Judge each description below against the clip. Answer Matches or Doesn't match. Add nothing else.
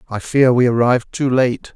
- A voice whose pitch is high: Doesn't match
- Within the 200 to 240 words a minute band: Matches